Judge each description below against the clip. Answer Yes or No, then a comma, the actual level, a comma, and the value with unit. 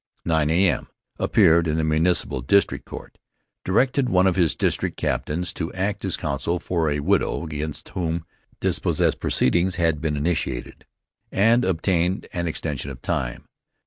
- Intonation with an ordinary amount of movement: Yes, average, 3.2 semitones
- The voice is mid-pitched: No, very low, 85 Hz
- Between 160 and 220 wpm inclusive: No, average, 145 wpm